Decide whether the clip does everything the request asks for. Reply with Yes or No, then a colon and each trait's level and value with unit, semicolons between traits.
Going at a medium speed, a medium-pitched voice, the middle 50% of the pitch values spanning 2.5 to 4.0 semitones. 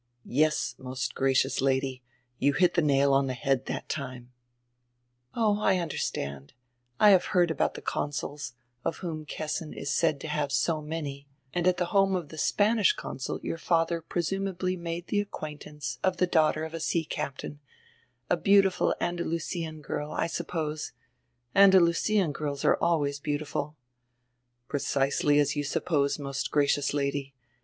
Yes: average, 150 wpm; medium, 155 Hz; average, 3.6 semitones